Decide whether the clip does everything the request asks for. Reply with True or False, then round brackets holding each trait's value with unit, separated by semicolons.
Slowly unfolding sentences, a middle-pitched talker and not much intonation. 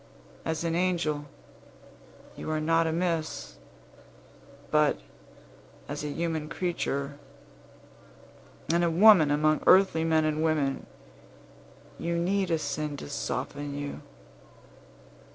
True (105 wpm; 160 Hz; 2.3 semitones)